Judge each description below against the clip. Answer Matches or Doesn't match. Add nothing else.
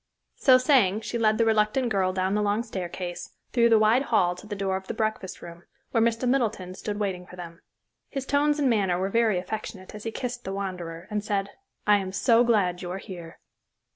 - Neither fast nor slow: Doesn't match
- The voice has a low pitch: Doesn't match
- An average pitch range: Matches